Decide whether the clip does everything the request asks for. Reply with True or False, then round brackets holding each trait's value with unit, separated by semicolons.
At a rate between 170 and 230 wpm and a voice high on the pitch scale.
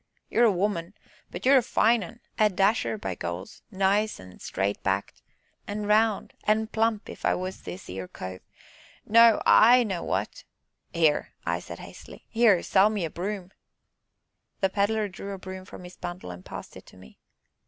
True (180 wpm; 195 Hz)